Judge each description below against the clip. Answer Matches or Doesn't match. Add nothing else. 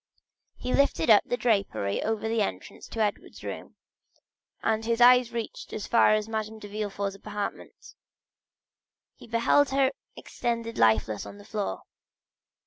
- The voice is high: Matches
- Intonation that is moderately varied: Doesn't match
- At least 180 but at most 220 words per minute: Doesn't match